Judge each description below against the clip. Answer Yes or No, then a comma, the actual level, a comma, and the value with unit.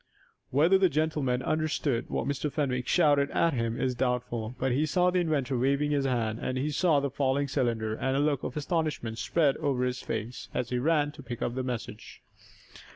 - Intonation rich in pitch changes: No, average, 3.3 semitones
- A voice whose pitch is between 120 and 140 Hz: Yes, low, 135 Hz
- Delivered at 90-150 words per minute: No, average, 200 wpm